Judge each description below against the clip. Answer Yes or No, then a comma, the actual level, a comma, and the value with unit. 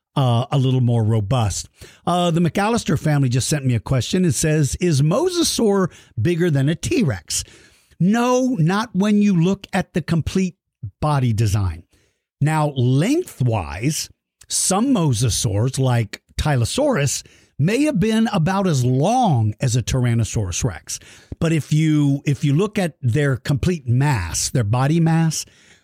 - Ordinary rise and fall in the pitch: No, wide, 6.3 semitones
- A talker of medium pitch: Yes, medium, 145 Hz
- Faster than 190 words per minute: No, average, 140 wpm